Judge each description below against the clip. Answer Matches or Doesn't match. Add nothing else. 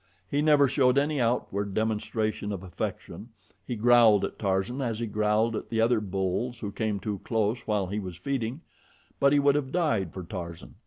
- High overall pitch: Doesn't match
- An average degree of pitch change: Matches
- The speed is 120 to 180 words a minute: Doesn't match